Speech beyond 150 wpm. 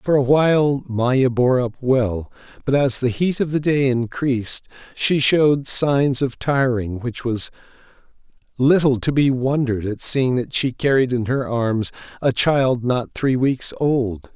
Yes: average, 165 wpm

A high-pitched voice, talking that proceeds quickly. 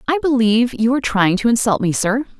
Yes: high, 230 Hz; fast, 225 wpm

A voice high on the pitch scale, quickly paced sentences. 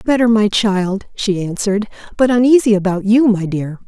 No: high, 210 Hz; average, 170 wpm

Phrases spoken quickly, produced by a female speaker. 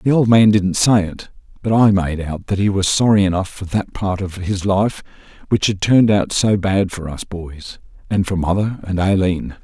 No: fast, 220 wpm; male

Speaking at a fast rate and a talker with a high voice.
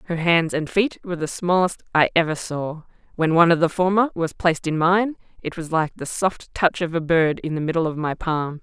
No: fast, 235 wpm; medium, 165 Hz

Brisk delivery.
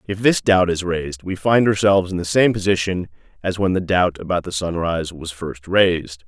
Yes: fast, 210 wpm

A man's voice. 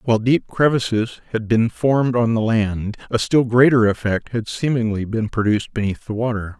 Yes: male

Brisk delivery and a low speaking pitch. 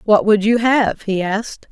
No: fast, 210 wpm; high, 210 Hz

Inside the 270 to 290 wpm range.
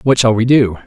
Yes: fast, 275 wpm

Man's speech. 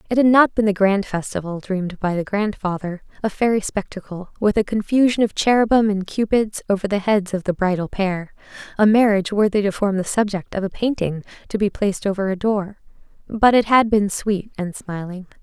No: female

